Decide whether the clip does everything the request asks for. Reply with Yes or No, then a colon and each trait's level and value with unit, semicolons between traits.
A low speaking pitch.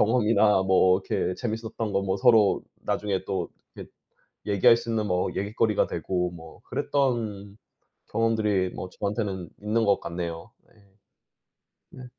Yes: low, 105 Hz